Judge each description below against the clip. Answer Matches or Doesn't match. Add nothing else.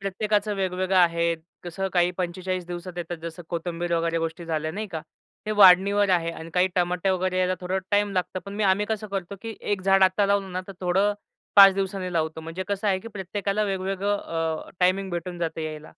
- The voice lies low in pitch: Doesn't match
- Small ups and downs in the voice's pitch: Matches